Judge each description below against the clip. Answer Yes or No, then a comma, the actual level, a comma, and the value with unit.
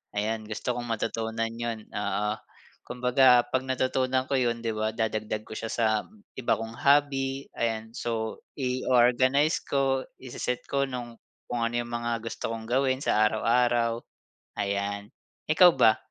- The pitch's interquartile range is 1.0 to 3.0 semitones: Yes, narrow, 2.5 semitones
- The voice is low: Yes, low, 120 Hz